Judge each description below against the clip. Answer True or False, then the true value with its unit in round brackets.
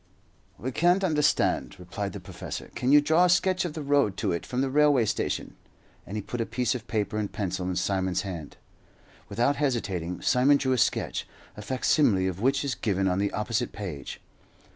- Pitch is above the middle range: False (115 Hz)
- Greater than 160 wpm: True (195 wpm)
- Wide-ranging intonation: True (6.7 semitones)